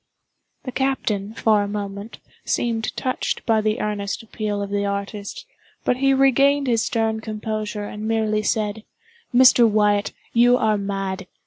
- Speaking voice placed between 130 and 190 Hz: No, high, 215 Hz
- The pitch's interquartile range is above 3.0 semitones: No, narrow, 2.4 semitones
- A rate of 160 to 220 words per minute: No, average, 145 wpm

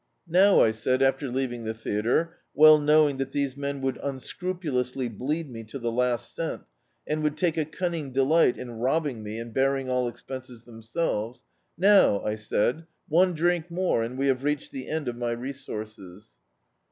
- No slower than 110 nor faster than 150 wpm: No, average, 175 wpm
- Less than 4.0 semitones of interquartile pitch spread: No, average, 4.5 semitones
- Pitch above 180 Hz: No, low, 135 Hz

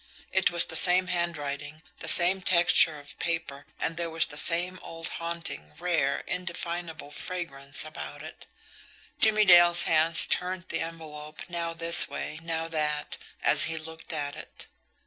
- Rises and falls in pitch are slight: Yes, narrow, 2.1 semitones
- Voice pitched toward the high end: No, medium, 165 Hz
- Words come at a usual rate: Yes, average, 150 wpm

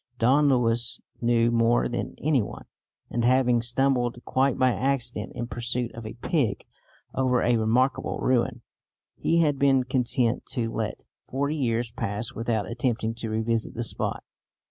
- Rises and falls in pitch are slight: Yes, narrow, 2.1 semitones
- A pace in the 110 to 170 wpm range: Yes, average, 150 wpm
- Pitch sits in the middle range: No, low, 120 Hz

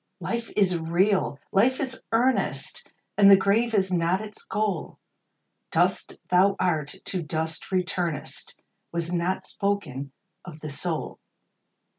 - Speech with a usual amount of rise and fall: Yes, average, 3.3 semitones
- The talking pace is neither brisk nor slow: No, slow, 125 wpm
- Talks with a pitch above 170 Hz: Yes, medium, 185 Hz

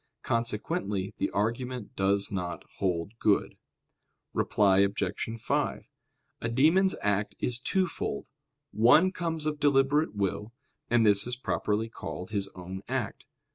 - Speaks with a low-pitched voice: Yes, low, 110 Hz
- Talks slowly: Yes, slow, 125 wpm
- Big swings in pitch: No, average, 4.7 semitones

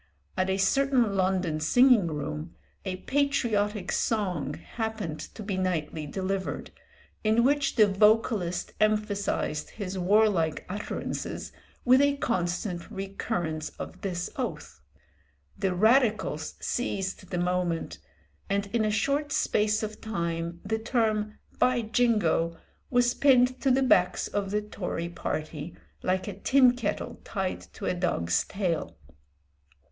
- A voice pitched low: No, high, 200 Hz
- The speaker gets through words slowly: Yes, slow, 125 wpm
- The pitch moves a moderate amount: Yes, average, 4.2 semitones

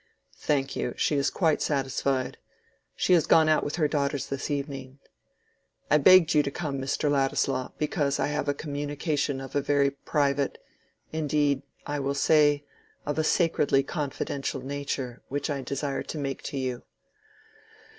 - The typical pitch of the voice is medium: Yes, medium, 145 Hz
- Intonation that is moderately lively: No, narrow, 1.5 semitones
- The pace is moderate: Yes, average, 155 wpm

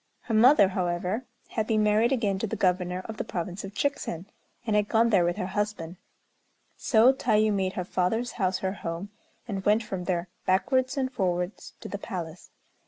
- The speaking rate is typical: Yes, average, 185 wpm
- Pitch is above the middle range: Yes, high, 200 Hz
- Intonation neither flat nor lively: Yes, average, 3.4 semitones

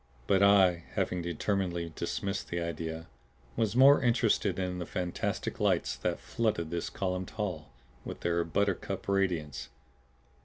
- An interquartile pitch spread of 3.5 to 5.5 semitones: No, average, 2.8 semitones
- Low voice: Yes, very low, 90 Hz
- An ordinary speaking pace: No, slow, 130 wpm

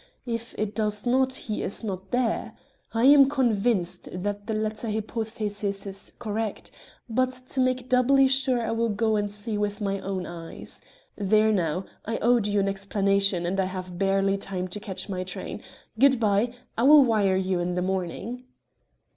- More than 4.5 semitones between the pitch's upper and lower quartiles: No, average, 3.1 semitones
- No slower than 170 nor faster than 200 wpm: Yes, average, 175 wpm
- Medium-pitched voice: No, high, 210 Hz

